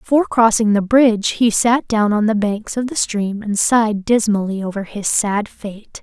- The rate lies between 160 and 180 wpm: No, average, 200 wpm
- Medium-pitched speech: No, high, 215 Hz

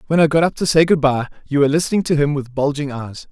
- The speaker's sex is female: No, male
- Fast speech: Yes, fast, 290 wpm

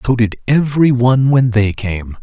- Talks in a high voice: No, low, 120 Hz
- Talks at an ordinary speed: Yes, average, 190 wpm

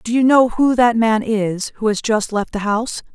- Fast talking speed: Yes, fast, 250 wpm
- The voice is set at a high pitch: Yes, high, 225 Hz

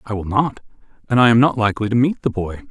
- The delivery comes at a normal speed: No, fast, 265 wpm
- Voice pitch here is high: No, low, 110 Hz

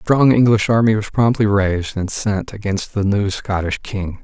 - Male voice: Yes, male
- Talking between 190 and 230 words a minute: Yes, average, 200 wpm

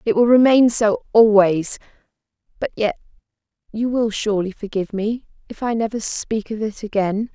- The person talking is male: No, female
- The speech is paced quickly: No, average, 155 wpm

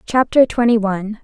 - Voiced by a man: No, female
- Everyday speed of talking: Yes, average, 145 wpm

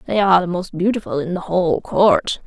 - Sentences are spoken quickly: Yes, fast, 220 wpm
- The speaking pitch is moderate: Yes, medium, 180 Hz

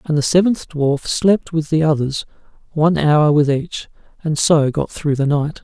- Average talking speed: Yes, average, 190 wpm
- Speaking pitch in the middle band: Yes, medium, 155 Hz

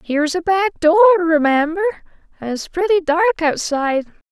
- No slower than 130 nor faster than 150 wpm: Yes, average, 140 wpm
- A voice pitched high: Yes, very high, 340 Hz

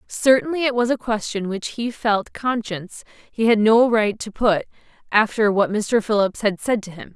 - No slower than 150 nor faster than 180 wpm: No, average, 195 wpm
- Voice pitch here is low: No, high, 220 Hz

